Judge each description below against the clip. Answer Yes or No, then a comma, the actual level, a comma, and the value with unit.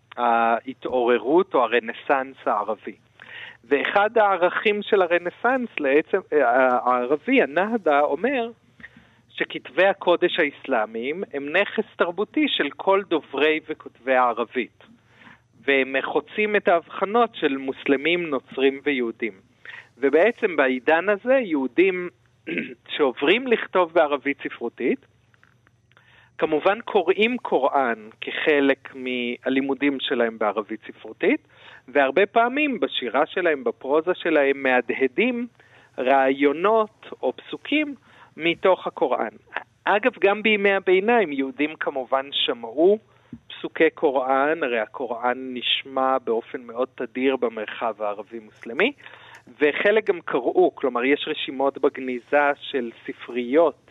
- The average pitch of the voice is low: No, medium, 145 Hz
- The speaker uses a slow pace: Yes, slow, 95 wpm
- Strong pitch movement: Yes, wide, 7.9 semitones